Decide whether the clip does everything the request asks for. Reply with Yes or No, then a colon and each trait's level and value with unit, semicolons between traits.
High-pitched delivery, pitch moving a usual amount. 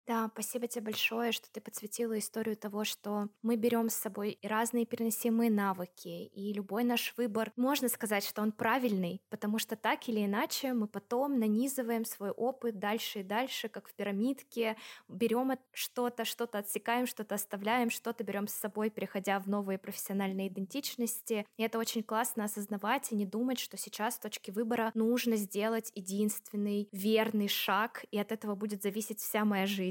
No: high, 220 Hz; narrow, 2.2 semitones